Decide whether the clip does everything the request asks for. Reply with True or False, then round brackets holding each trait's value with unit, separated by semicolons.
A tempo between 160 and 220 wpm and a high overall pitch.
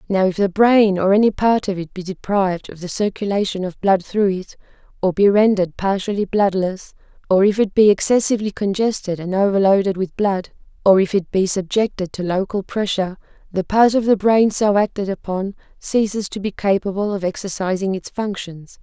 True (180 wpm; 195 Hz)